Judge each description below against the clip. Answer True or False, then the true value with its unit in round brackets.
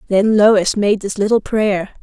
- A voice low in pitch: False (205 Hz)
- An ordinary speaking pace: True (180 wpm)